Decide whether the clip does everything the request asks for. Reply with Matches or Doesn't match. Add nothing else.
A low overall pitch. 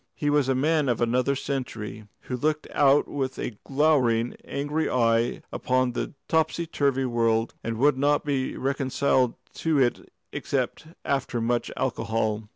Matches